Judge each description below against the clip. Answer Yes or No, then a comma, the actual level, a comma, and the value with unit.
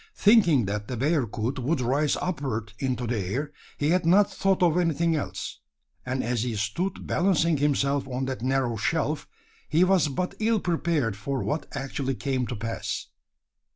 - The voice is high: No, medium, 140 Hz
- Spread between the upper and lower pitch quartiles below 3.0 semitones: No, average, 5.2 semitones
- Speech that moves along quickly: No, average, 165 wpm